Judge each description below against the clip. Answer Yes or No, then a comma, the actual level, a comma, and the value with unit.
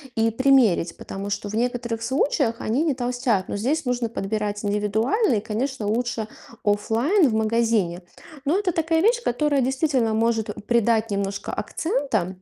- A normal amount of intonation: Yes, average, 4.1 semitones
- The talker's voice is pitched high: Yes, high, 230 Hz